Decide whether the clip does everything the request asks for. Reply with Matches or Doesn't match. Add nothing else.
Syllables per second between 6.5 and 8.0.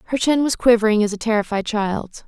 Doesn't match